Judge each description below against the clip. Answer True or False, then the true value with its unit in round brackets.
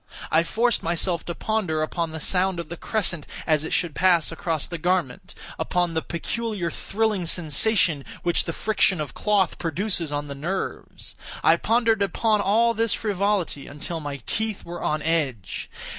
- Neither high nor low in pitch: True (175 Hz)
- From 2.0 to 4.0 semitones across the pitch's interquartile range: False (4.6 semitones)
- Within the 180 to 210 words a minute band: False (160 wpm)